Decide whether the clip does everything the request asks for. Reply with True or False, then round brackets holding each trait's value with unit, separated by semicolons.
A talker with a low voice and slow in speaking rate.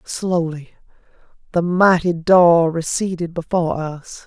False (170 Hz; 100 wpm)